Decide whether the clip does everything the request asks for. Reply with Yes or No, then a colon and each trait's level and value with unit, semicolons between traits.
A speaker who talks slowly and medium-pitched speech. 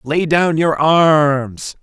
Yes: slow, 130 wpm; medium, 155 Hz